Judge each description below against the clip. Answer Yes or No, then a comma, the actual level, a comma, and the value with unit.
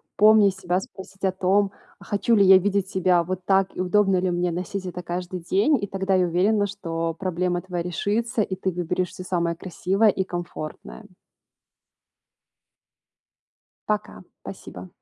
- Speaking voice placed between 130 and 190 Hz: Yes, medium, 185 Hz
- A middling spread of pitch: No, narrow, 2.0 semitones